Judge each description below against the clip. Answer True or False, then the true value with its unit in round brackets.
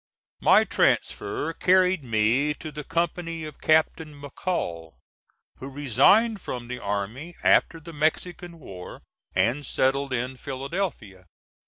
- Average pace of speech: False (120 wpm)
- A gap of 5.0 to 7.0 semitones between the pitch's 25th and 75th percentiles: True (5.3 semitones)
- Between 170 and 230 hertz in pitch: False (145 Hz)